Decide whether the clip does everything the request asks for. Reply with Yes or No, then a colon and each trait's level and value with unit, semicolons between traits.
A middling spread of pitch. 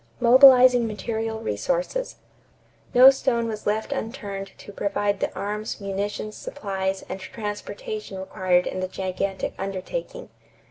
Yes: average, 4.3 semitones